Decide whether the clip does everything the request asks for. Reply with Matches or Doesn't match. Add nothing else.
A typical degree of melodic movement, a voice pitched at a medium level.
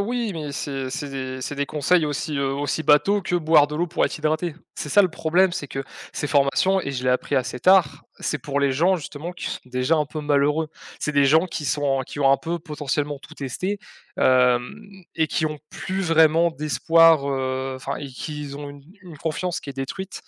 Matches